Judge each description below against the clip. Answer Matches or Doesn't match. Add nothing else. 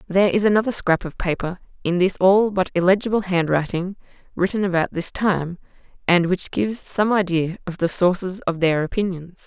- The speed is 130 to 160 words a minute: Doesn't match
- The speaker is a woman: Matches